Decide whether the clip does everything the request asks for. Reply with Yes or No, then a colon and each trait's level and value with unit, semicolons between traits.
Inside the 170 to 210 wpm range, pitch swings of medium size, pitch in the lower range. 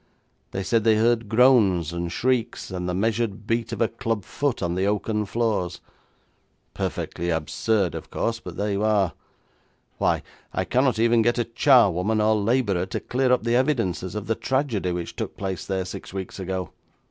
Yes: average, 180 wpm; average, 4.0 semitones; low, 105 Hz